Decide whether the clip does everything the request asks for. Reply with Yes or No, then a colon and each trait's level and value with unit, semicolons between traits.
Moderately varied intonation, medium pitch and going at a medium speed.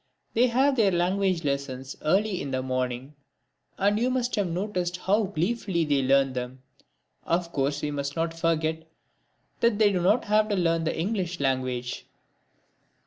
No: wide, 6.6 semitones; medium, 170 Hz; average, 160 wpm